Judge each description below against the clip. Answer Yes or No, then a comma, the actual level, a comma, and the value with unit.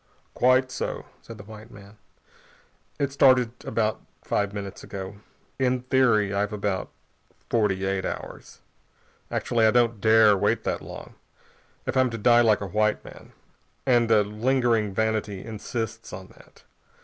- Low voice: Yes, low, 110 Hz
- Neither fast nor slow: Yes, average, 145 wpm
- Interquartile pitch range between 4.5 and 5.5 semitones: No, average, 2.8 semitones